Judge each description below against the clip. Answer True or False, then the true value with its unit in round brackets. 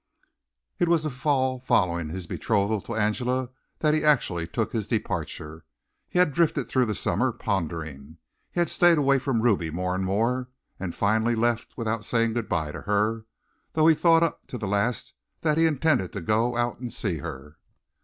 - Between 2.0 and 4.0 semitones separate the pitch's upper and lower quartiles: False (5.6 semitones)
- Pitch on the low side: True (115 Hz)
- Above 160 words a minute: True (185 wpm)